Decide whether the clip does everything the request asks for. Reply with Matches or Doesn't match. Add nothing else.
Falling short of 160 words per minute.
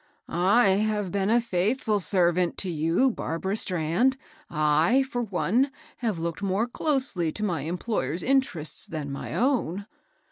Matches